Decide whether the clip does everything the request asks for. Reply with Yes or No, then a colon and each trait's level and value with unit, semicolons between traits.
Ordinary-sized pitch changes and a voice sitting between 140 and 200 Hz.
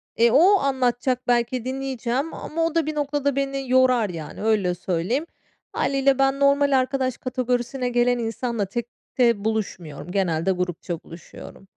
No: average, 4.3 semitones; high, 245 Hz